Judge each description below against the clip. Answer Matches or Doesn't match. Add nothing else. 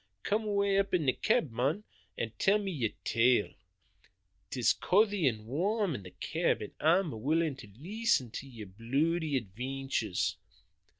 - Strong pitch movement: Matches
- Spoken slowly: Doesn't match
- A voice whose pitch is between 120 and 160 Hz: Matches